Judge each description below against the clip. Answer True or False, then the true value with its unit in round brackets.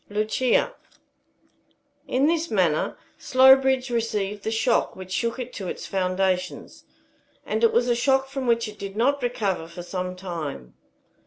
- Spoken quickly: False (150 wpm)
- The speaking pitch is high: True (220 Hz)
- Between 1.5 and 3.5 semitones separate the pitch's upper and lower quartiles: False (5.3 semitones)